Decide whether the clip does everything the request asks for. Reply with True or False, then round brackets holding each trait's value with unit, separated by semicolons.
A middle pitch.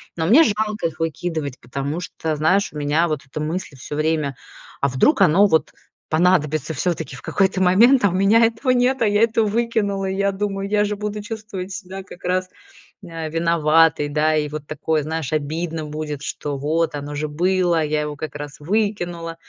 True (165 Hz)